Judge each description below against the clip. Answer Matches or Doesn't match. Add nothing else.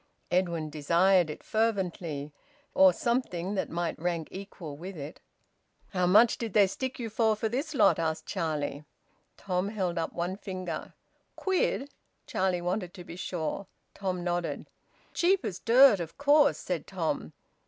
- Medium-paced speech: Matches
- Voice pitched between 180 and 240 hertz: Matches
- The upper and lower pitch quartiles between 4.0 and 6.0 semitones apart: Matches